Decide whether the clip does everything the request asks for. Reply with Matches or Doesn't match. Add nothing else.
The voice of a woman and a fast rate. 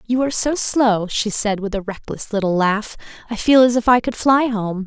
Matches